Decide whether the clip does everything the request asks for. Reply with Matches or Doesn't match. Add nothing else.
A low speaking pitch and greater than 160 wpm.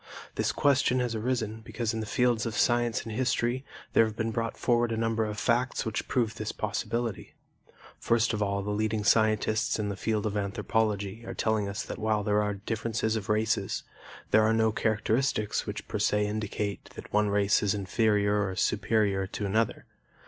Matches